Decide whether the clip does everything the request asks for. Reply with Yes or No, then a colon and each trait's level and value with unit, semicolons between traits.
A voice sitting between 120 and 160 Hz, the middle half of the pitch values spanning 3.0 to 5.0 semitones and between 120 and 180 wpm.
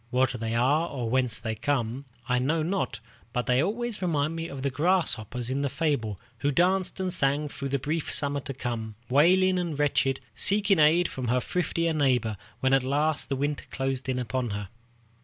No: medium, 140 Hz; average, 4.5 semitones; average, 195 wpm